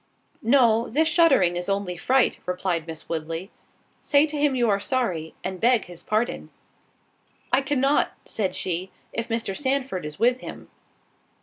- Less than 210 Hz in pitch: No, high, 225 Hz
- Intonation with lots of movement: Yes, wide, 6.7 semitones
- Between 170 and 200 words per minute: No, average, 145 wpm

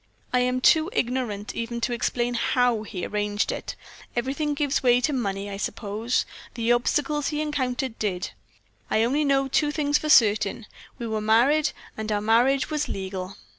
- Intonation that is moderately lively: Yes, average, 4.3 semitones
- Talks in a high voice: Yes, high, 240 Hz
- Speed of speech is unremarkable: Yes, average, 170 wpm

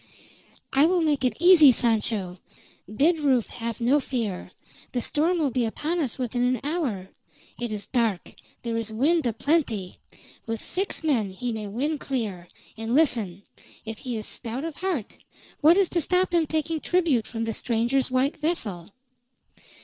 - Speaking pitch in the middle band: No, very high, 250 Hz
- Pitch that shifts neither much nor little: No, wide, 5.8 semitones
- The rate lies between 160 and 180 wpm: Yes, average, 165 wpm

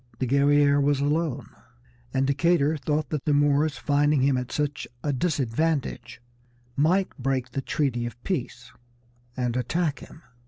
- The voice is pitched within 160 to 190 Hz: No, medium, 145 Hz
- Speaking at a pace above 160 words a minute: No, average, 145 wpm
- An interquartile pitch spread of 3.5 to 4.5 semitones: No, narrow, 2.4 semitones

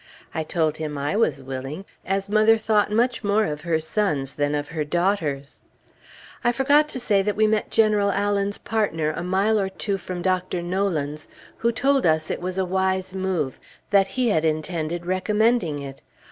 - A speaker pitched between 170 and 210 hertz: Yes, high, 190 Hz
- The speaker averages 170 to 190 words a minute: Yes, average, 180 wpm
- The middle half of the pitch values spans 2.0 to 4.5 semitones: No, average, 5.1 semitones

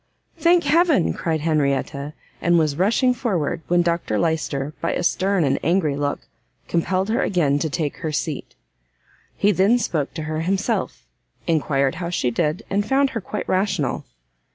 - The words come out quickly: No, average, 160 wpm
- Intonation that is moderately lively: Yes, average, 4.6 semitones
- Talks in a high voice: No, medium, 170 Hz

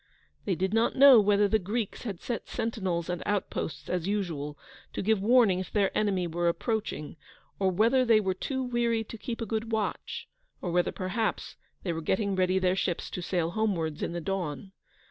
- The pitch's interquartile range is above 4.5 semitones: No, average, 3.8 semitones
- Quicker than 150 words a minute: Yes, average, 190 wpm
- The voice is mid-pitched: No, high, 195 Hz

